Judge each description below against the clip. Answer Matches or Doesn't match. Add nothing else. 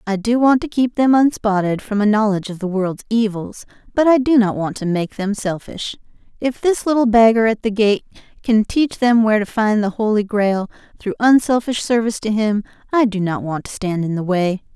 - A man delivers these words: Doesn't match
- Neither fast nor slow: Doesn't match